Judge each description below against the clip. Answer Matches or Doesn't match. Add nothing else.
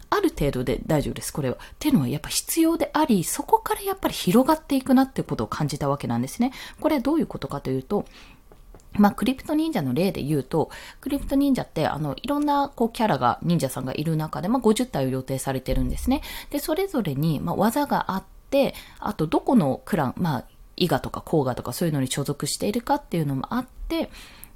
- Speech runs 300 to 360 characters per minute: Doesn't match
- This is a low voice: Doesn't match